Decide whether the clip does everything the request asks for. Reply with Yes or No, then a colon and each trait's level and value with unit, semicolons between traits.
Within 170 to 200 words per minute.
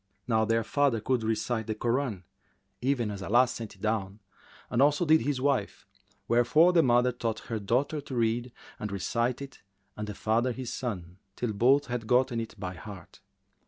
Yes: average, 180 wpm